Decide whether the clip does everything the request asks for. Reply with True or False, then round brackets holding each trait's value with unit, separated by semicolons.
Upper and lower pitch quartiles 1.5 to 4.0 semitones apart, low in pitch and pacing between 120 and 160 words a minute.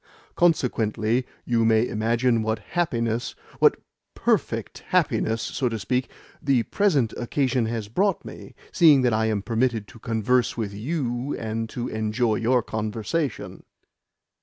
True (2.5 semitones; 115 Hz; 135 wpm)